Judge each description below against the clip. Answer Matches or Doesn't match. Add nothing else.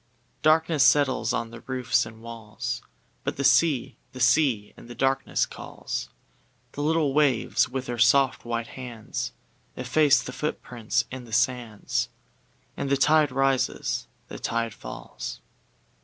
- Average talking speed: Doesn't match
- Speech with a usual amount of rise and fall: Matches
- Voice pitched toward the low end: Matches